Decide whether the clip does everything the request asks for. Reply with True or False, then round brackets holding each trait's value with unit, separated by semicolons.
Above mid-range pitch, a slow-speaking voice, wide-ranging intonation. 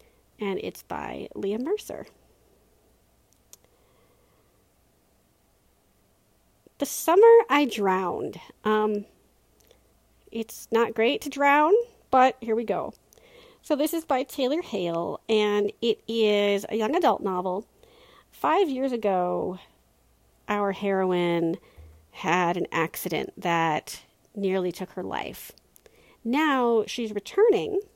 True (220 Hz; 105 wpm; 7.3 semitones)